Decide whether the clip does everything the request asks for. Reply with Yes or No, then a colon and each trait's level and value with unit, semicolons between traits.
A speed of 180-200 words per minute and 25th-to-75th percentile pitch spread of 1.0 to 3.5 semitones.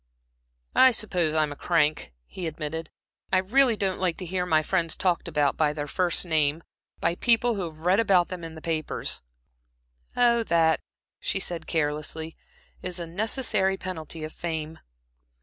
No: average, 165 wpm; average, 3.1 semitones